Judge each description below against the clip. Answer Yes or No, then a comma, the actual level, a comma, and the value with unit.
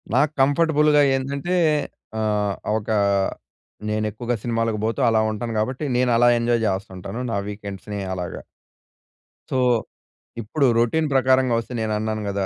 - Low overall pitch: Yes, low, 115 Hz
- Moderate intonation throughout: Yes, average, 3.8 semitones